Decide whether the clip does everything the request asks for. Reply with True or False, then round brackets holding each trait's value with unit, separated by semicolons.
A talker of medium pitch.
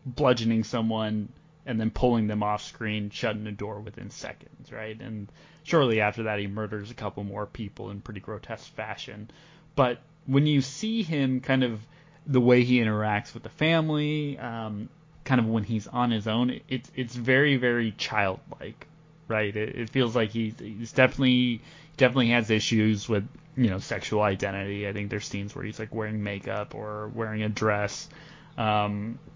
False (115 Hz)